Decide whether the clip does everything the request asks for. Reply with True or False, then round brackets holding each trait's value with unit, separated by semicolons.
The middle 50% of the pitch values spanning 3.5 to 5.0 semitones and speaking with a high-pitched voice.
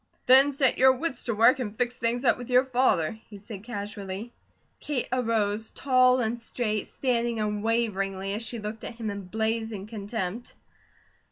False (3.1 semitones; 230 Hz)